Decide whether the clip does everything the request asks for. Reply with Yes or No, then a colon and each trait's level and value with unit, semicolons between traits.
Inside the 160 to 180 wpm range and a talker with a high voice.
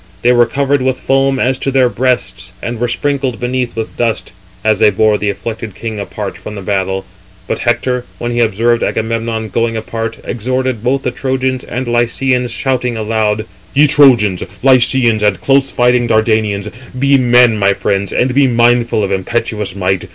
No: average, 175 wpm; low, 120 Hz